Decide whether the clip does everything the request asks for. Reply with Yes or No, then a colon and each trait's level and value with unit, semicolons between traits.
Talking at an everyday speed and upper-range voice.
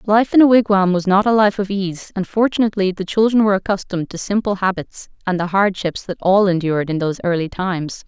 No: fast, 215 wpm; high, 195 Hz